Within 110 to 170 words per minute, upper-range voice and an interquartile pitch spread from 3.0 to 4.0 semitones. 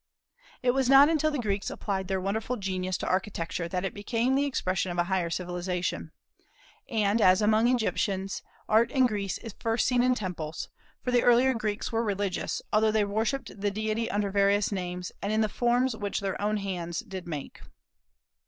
No: average, 185 wpm; high, 205 Hz; average, 3.7 semitones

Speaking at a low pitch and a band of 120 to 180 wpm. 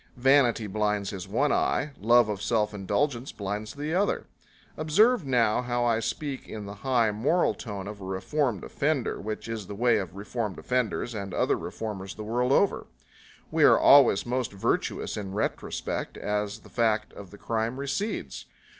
Yes: low, 115 Hz; average, 170 wpm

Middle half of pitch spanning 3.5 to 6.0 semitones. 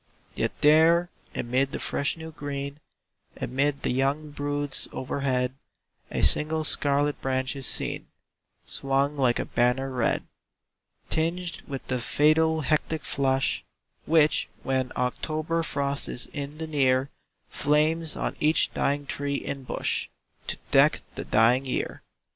No: narrow, 2.5 semitones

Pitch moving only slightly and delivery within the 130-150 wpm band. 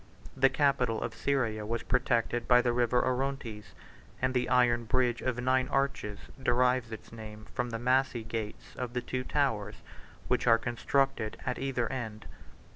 No: narrow, 2.2 semitones; average, 165 wpm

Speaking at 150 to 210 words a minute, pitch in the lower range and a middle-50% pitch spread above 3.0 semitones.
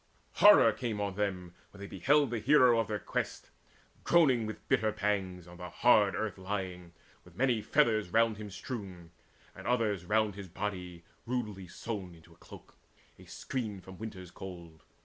Yes: average, 170 wpm; low, 105 Hz; average, 3.8 semitones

